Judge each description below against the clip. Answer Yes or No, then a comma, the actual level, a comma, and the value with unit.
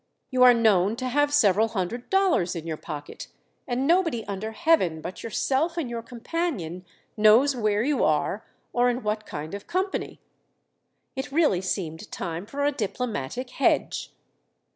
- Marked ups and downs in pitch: Yes, wide, 6.5 semitones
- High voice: Yes, high, 230 Hz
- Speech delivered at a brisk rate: No, average, 155 wpm